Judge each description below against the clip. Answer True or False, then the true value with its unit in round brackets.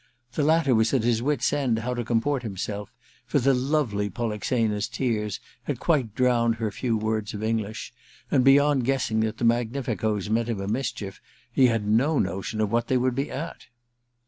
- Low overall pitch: True (115 Hz)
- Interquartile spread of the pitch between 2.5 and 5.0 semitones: True (3.3 semitones)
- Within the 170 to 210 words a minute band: True (180 wpm)